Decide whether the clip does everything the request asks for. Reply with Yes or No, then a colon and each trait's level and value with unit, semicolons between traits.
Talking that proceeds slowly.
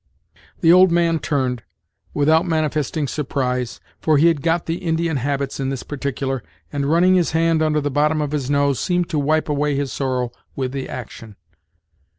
No: average, 175 wpm